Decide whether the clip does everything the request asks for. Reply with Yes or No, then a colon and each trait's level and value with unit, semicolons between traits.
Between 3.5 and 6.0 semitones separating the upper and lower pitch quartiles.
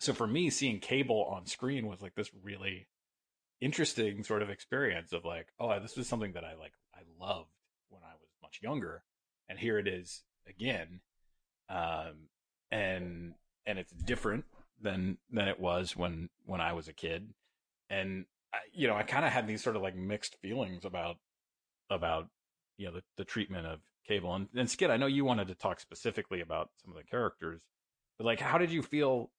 Yes: average, 4.0 semitones